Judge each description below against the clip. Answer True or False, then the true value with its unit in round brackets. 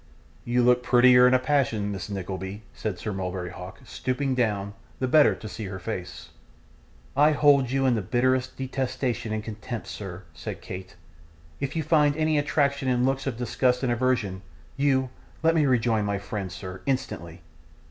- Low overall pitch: True (125 Hz)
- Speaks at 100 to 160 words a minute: False (170 wpm)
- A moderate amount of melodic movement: True (4.8 semitones)